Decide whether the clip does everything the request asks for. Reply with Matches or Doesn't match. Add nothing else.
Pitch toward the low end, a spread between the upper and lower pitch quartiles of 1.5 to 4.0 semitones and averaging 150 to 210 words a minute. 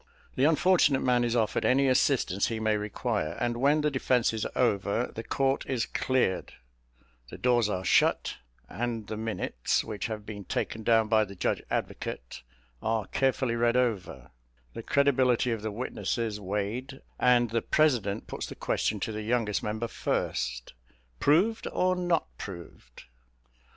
Matches